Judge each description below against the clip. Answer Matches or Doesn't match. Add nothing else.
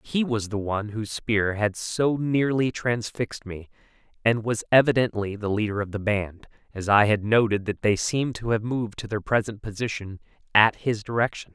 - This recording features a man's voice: Matches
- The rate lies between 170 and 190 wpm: Matches